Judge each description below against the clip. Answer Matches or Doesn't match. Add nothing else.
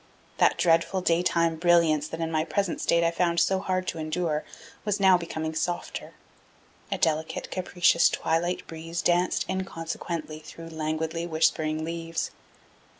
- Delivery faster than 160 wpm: Doesn't match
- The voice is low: Doesn't match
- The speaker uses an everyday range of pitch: Doesn't match